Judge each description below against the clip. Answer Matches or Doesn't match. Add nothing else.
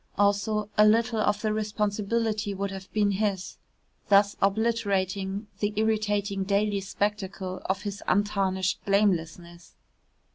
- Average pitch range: Doesn't match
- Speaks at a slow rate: Matches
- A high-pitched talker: Matches